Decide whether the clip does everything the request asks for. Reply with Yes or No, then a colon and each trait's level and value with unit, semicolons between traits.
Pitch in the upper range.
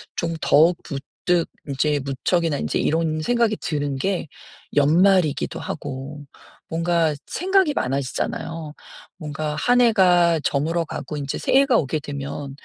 No: medium, 160 Hz